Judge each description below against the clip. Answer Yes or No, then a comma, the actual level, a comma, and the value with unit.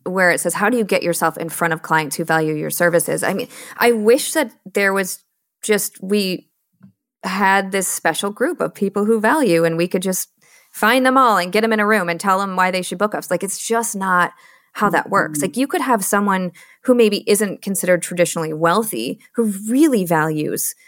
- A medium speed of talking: No, fast, 215 wpm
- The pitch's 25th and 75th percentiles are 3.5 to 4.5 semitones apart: Yes, average, 4.1 semitones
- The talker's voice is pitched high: Yes, high, 195 Hz